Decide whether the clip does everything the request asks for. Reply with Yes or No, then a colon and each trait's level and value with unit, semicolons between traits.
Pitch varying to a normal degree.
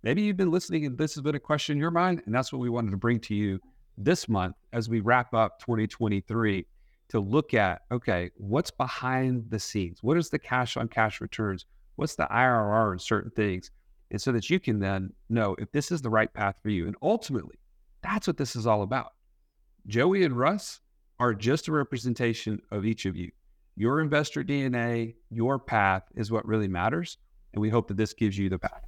Yes: average, 4.7 semitones